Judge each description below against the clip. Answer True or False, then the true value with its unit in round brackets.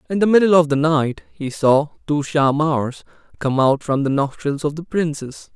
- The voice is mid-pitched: True (150 Hz)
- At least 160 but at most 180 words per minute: False (195 wpm)